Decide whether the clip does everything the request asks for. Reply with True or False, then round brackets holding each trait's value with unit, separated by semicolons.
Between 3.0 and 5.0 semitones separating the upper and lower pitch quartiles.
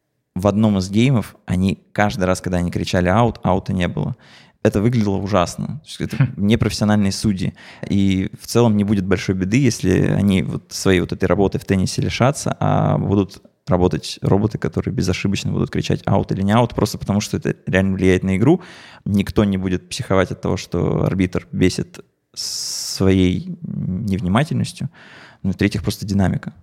False (2.6 semitones)